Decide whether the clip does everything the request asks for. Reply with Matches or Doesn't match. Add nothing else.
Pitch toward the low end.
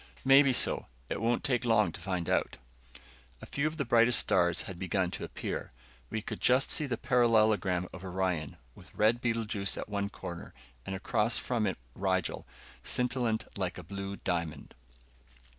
Matches